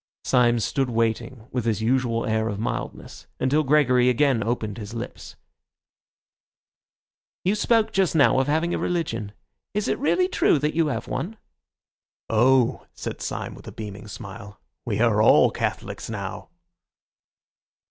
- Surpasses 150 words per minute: No, average, 145 wpm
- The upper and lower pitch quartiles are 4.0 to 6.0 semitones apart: Yes, average, 5.2 semitones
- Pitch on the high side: No, low, 125 Hz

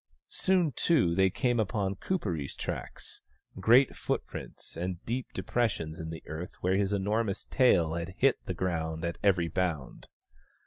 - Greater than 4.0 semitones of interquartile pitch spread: Yes, wide, 5.4 semitones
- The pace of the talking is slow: No, average, 150 wpm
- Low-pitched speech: Yes, very low, 95 Hz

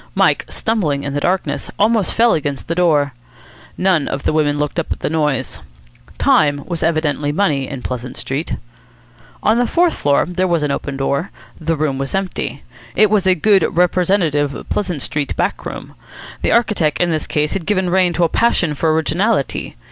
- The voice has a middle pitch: Yes, medium, 160 Hz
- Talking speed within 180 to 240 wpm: Yes, average, 185 wpm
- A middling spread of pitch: Yes, average, 4.5 semitones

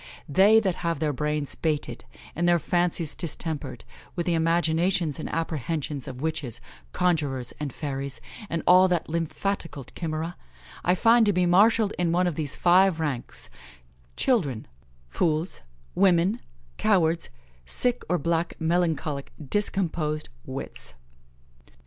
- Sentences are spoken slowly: Yes, slow, 125 wpm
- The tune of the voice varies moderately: Yes, average, 3.1 semitones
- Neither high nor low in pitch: Yes, medium, 165 Hz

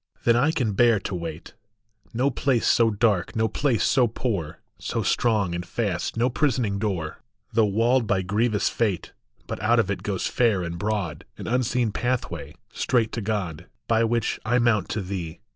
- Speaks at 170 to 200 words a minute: Yes, average, 175 wpm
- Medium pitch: No, low, 110 Hz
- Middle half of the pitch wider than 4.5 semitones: No, average, 3.8 semitones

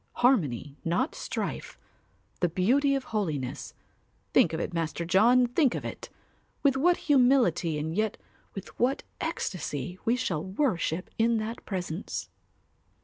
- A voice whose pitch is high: Yes, high, 200 Hz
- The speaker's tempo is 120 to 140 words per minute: Yes, slow, 135 wpm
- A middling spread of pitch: No, wide, 7.1 semitones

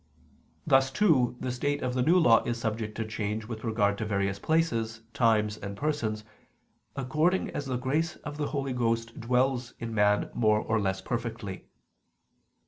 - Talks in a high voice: No, low, 115 Hz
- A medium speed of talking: Yes, average, 165 wpm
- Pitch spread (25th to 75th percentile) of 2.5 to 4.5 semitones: Yes, average, 3.8 semitones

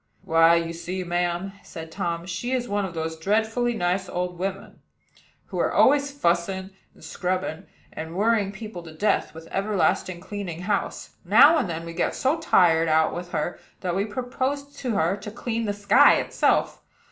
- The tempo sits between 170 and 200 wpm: Yes, average, 175 wpm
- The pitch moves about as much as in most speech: Yes, average, 4.1 semitones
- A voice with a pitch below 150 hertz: No, high, 190 Hz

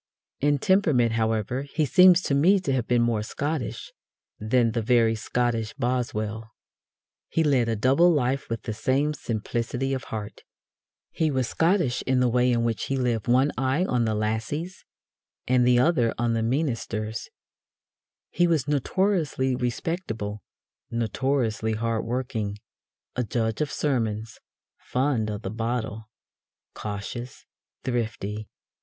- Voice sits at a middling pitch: No, low, 120 Hz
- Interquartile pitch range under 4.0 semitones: Yes, average, 3.6 semitones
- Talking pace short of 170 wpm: Yes, average, 140 wpm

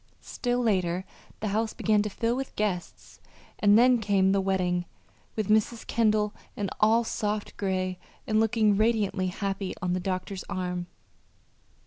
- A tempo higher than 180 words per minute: No, average, 145 wpm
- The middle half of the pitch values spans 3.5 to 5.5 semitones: No, average, 2.7 semitones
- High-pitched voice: Yes, high, 205 Hz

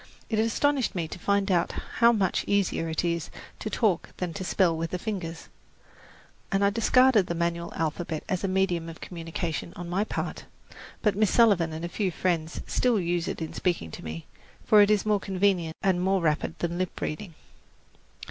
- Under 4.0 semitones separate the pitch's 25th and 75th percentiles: Yes, average, 3.3 semitones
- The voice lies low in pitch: No, medium, 180 Hz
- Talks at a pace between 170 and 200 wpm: Yes, average, 185 wpm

